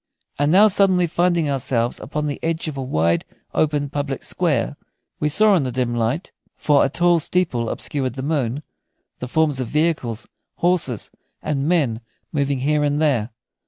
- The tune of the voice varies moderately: Yes, average, 4.1 semitones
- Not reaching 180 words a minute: Yes, average, 165 wpm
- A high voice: No, medium, 145 Hz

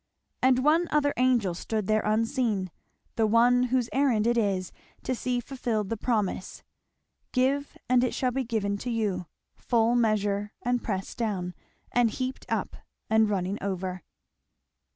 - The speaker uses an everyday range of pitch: Yes, average, 3.7 semitones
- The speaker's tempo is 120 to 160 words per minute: Yes, average, 150 wpm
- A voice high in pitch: Yes, high, 230 Hz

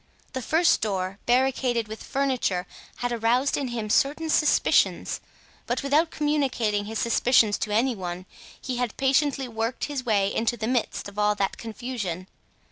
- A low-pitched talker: No, high, 240 Hz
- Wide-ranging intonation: No, average, 4.1 semitones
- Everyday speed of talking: Yes, average, 155 wpm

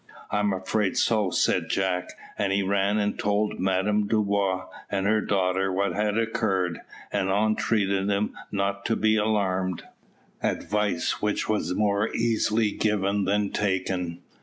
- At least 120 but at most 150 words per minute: Yes, average, 140 wpm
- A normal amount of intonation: No, narrow, 1.7 semitones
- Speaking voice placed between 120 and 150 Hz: No, low, 100 Hz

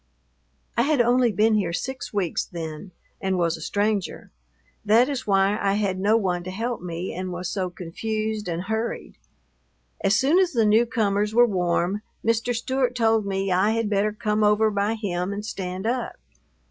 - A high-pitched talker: Yes, high, 210 Hz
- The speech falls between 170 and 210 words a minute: Yes, average, 175 wpm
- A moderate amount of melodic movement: Yes, average, 3.3 semitones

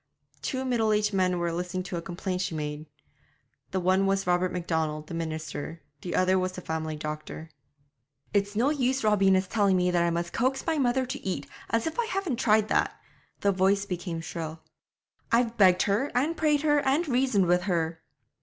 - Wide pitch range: Yes, wide, 5.7 semitones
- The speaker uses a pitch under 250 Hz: Yes, high, 190 Hz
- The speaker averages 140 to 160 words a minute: No, average, 190 wpm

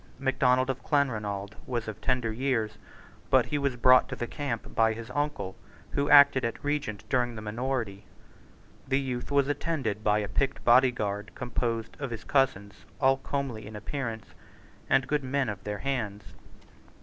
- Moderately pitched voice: No, low, 125 Hz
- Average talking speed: Yes, average, 170 wpm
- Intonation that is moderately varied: Yes, average, 4.0 semitones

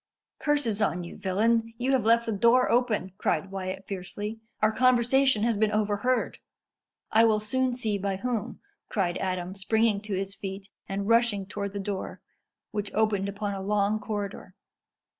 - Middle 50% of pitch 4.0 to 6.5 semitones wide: No, average, 2.8 semitones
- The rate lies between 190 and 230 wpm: No, average, 160 wpm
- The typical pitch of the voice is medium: No, high, 210 Hz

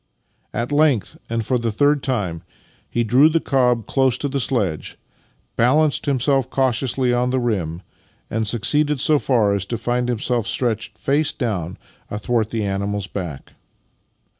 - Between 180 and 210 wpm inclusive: No, average, 150 wpm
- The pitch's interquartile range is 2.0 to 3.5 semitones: No, average, 4.2 semitones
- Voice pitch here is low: Yes, low, 120 Hz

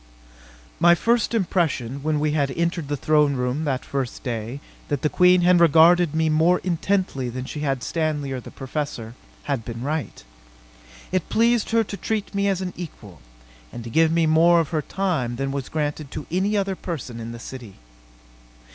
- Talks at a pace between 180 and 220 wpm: Yes, average, 185 wpm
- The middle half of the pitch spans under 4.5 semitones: No, average, 4.8 semitones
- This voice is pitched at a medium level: Yes, medium, 155 Hz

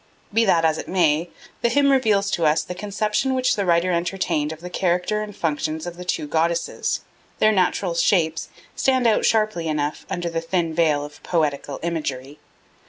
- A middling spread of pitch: Yes, average, 4.2 semitones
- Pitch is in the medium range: Yes, medium, 170 Hz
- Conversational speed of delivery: Yes, average, 180 wpm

